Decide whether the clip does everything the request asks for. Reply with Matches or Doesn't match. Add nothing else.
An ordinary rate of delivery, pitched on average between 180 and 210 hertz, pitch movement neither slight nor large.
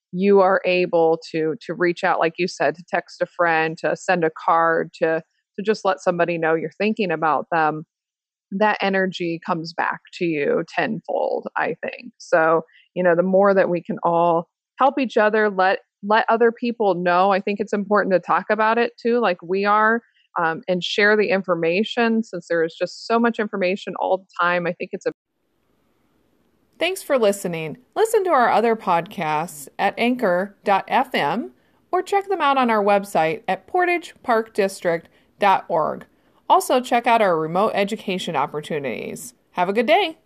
Matches